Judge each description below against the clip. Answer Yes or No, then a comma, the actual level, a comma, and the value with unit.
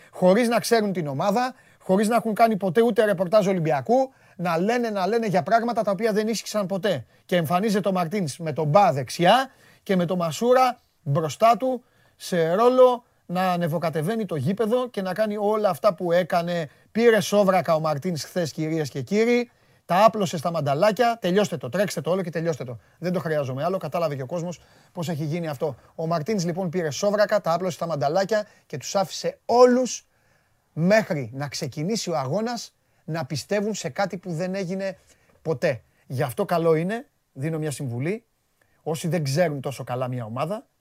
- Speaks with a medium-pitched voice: Yes, medium, 180 Hz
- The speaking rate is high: Yes, fast, 180 wpm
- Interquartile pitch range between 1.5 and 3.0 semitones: No, average, 5.1 semitones